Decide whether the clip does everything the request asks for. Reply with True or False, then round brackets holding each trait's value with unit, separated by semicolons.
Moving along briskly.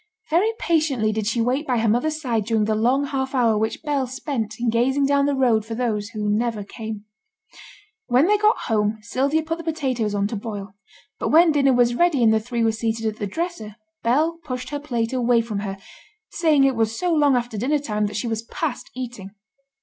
True (215 wpm)